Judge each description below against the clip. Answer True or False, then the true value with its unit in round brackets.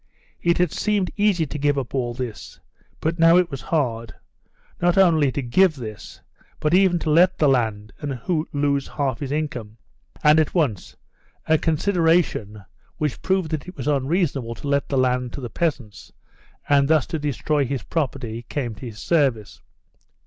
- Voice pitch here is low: False (145 Hz)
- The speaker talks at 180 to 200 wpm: False (170 wpm)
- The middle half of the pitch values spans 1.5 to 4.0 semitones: False (4.7 semitones)